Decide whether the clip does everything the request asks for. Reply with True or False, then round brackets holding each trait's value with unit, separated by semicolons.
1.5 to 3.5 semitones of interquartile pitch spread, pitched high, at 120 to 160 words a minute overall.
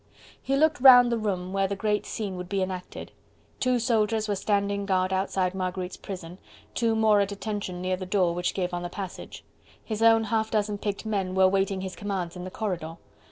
False (2.8 semitones; 195 Hz; 205 wpm)